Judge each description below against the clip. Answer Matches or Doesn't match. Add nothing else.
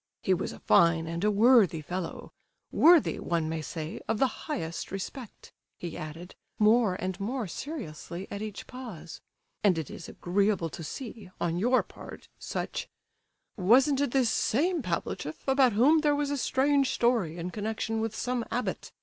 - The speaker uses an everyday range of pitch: Doesn't match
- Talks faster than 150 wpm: Matches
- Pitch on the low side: Doesn't match